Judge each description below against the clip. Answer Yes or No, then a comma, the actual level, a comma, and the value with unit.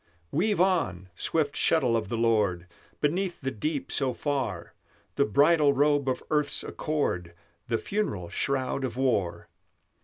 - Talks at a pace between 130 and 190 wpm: Yes, average, 140 wpm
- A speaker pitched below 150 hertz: Yes, low, 135 Hz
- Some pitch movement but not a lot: No, wide, 5.9 semitones